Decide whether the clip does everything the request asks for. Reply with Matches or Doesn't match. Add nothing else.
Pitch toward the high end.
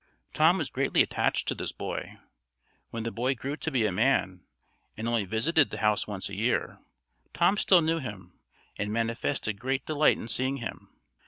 Doesn't match